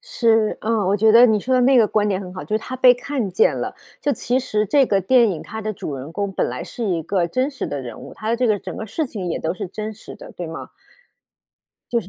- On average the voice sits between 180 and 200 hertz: No, high, 215 Hz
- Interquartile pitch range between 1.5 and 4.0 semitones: No, average, 4.4 semitones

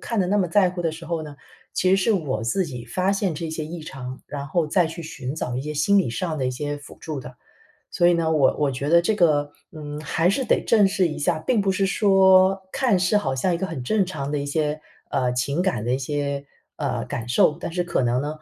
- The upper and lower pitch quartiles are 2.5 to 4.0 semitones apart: No, average, 4.7 semitones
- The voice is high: No, medium, 160 Hz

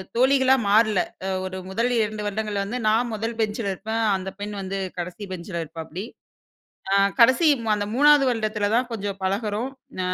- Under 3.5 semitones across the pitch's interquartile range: Yes, average, 3.0 semitones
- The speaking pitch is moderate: No, high, 210 Hz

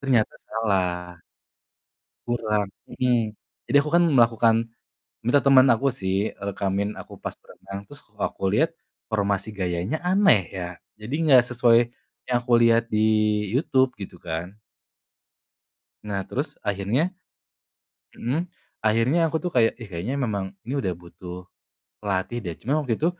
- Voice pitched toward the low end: Yes, low, 110 Hz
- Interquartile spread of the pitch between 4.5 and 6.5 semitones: Yes, average, 4.9 semitones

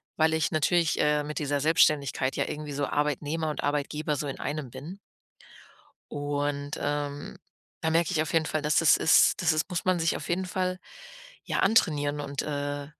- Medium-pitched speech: Yes, medium, 150 Hz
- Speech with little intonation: Yes, narrow, 1.8 semitones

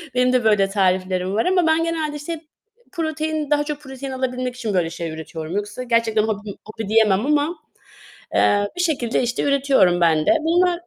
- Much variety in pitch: Yes, wide, 6.8 semitones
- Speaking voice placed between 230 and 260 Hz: Yes, very high, 250 Hz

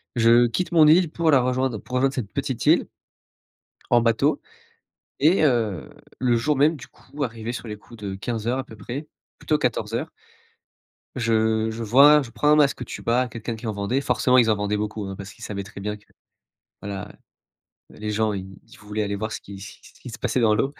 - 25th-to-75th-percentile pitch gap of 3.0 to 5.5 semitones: Yes, average, 3.7 semitones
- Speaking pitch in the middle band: No, low, 115 Hz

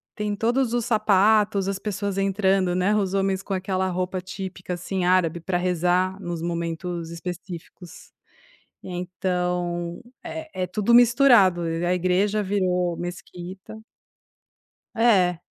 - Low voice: No, medium, 185 Hz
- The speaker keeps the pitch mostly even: Yes, narrow, 2.0 semitones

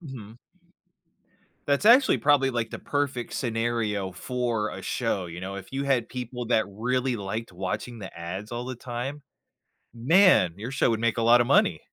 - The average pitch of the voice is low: Yes, low, 120 Hz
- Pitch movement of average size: Yes, average, 3.4 semitones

